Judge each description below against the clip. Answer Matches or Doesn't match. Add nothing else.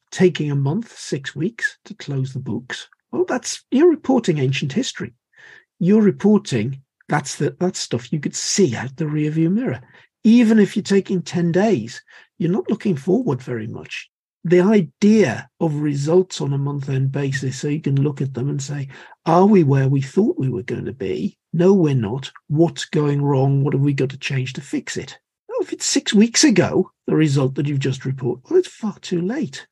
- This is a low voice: Doesn't match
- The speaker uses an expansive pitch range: Matches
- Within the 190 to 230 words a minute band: Matches